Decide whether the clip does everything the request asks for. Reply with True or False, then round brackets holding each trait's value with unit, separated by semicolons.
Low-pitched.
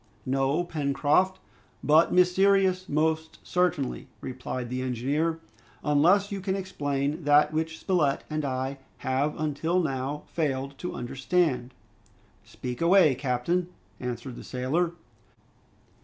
False (150 Hz)